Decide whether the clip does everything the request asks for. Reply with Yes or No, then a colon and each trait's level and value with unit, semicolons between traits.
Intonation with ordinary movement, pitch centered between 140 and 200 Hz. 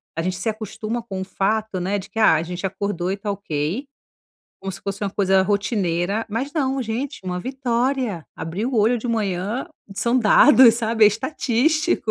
No: average, 4.0 semitones; high, 210 Hz